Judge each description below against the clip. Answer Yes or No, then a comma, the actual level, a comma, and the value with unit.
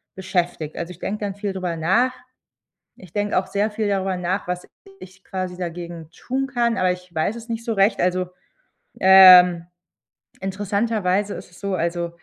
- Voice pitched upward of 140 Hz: Yes, high, 190 Hz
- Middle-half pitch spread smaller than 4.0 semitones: Yes, narrow, 2.4 semitones